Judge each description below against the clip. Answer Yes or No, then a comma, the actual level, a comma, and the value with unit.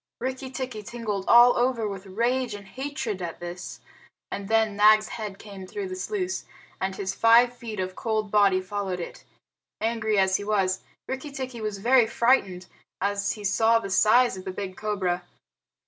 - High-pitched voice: Yes, high, 215 Hz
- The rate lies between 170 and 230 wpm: Yes, average, 175 wpm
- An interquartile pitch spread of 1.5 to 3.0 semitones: No, average, 3.7 semitones